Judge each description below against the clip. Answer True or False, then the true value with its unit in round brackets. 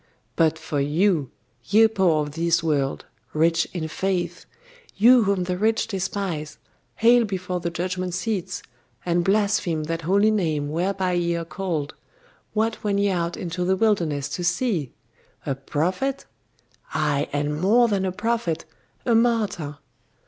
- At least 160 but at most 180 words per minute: False (145 wpm)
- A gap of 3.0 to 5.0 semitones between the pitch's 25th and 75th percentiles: True (4.1 semitones)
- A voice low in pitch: False (180 Hz)